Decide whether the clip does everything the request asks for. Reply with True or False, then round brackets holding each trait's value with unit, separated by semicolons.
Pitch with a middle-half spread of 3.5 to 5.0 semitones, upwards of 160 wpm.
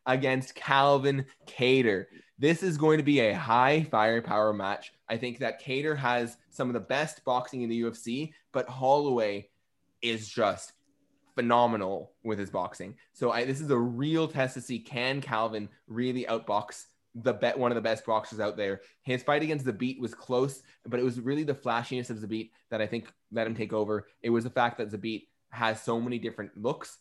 False (2.9 semitones; 200 wpm)